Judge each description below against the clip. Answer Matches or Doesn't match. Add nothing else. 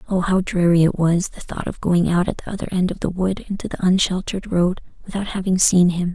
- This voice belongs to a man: Doesn't match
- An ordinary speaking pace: Doesn't match